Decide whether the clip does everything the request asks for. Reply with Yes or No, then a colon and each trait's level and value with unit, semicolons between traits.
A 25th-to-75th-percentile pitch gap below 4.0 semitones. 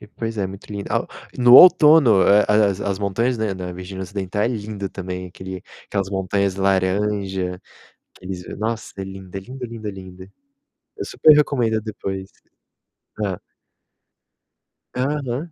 Yes: average, 3.0 semitones